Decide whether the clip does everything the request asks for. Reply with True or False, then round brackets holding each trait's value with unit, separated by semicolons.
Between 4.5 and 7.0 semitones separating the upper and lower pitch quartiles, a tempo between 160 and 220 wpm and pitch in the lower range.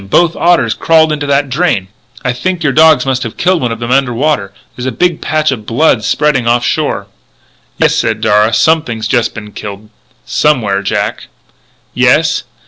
True (5.5 semitones; 180 wpm; 130 Hz)